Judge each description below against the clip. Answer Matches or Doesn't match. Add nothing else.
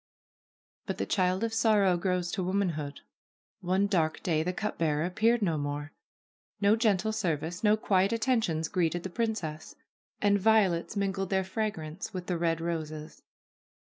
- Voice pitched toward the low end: Doesn't match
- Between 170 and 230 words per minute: Doesn't match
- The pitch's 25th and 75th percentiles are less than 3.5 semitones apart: Doesn't match